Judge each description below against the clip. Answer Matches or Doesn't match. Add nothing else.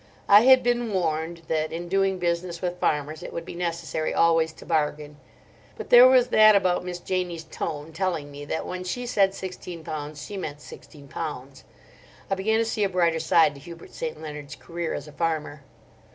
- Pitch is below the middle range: Doesn't match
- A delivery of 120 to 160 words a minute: Doesn't match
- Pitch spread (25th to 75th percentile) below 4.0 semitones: Matches